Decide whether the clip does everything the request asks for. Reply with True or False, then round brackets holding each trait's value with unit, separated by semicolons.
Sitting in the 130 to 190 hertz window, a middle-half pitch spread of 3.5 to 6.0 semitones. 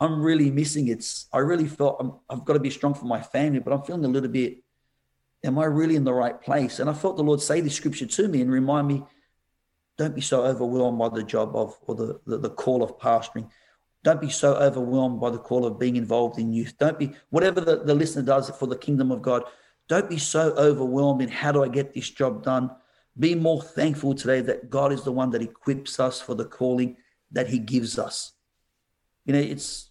False (135 Hz; 2.8 semitones)